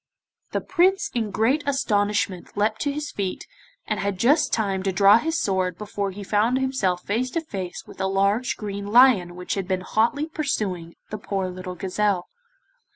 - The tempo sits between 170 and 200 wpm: Yes, average, 175 wpm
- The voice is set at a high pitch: Yes, high, 205 Hz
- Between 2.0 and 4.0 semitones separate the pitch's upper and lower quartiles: No, average, 4.8 semitones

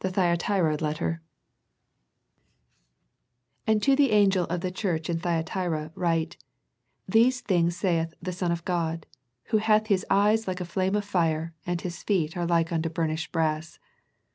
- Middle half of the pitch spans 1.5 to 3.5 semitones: Yes, average, 2.9 semitones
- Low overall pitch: No, medium, 175 Hz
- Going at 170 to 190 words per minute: No, average, 160 wpm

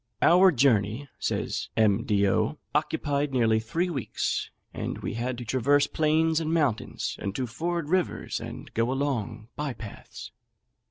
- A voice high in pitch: No, low, 135 Hz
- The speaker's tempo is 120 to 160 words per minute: Yes, average, 145 wpm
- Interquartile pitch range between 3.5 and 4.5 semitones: No, wide, 5.4 semitones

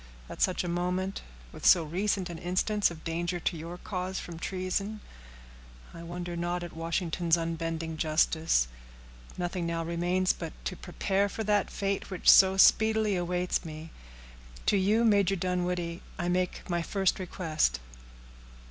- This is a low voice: No, medium, 180 Hz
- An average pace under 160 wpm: Yes, average, 150 wpm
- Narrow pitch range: Yes, narrow, 2.1 semitones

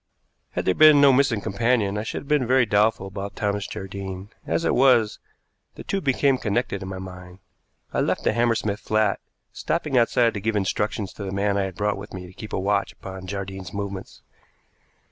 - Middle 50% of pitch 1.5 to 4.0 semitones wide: Yes, average, 3.5 semitones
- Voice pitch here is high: No, low, 105 Hz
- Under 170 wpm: No, average, 200 wpm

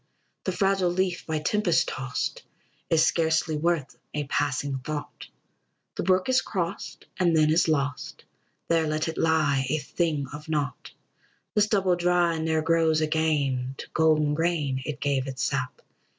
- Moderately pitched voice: Yes, medium, 160 Hz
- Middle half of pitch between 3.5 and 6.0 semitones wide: No, average, 2.9 semitones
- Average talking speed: Yes, average, 150 wpm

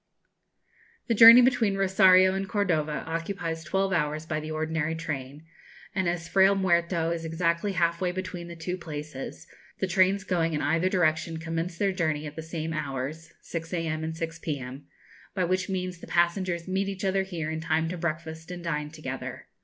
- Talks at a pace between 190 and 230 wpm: No, average, 180 wpm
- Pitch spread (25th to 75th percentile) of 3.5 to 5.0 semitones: No, average, 2.8 semitones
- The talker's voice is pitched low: No, medium, 170 Hz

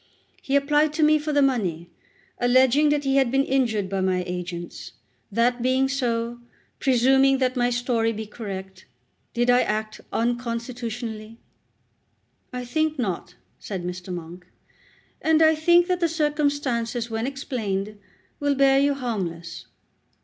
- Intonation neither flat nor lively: Yes, average, 4.5 semitones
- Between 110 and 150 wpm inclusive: Yes, average, 140 wpm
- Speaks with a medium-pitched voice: No, high, 245 Hz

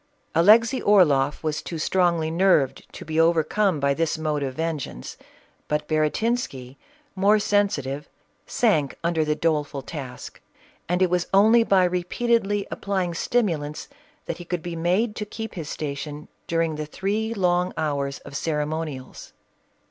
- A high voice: No, medium, 165 Hz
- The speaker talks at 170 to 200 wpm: No, average, 145 wpm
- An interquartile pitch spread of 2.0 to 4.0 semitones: No, average, 4.6 semitones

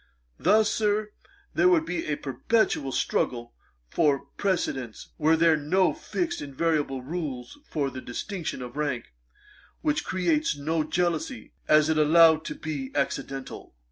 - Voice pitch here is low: No, medium, 155 Hz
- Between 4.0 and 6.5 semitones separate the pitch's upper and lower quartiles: Yes, average, 5.1 semitones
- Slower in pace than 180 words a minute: Yes, average, 140 wpm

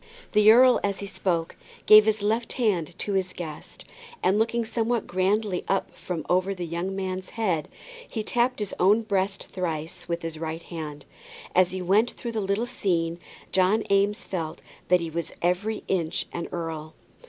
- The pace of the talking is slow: No, average, 170 wpm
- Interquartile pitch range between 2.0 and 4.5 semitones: Yes, average, 3.9 semitones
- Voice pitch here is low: No, high, 190 Hz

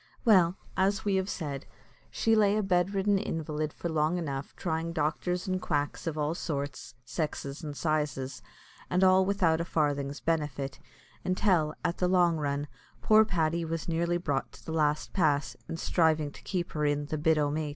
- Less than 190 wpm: Yes, average, 180 wpm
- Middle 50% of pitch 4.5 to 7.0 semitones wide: No, average, 3.3 semitones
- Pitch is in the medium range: Yes, medium, 160 Hz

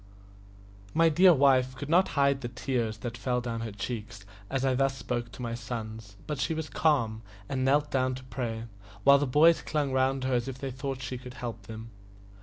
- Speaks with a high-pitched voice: No, low, 130 Hz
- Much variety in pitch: No, average, 2.8 semitones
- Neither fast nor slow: No, fast, 210 wpm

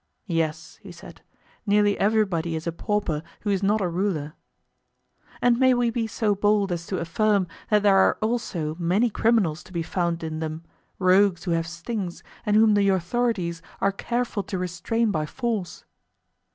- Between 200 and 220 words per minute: No, average, 170 wpm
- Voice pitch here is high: Yes, high, 195 Hz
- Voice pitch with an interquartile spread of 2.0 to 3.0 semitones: No, average, 4.2 semitones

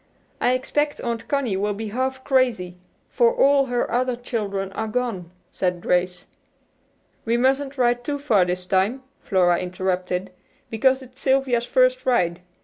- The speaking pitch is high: Yes, high, 240 Hz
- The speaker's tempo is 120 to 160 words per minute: Yes, average, 145 wpm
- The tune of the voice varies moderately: No, wide, 5.8 semitones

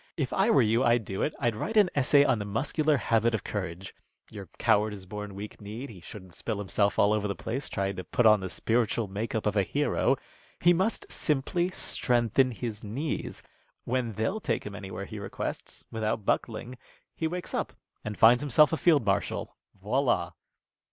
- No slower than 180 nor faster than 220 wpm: Yes, average, 190 wpm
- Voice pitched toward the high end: No, low, 110 Hz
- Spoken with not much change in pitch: No, average, 4.7 semitones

